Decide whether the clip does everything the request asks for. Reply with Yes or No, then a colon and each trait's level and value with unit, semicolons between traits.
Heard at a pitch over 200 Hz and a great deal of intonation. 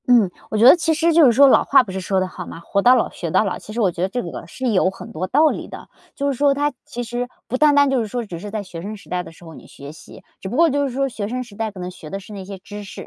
Yes: high, 215 Hz; wide, 5.9 semitones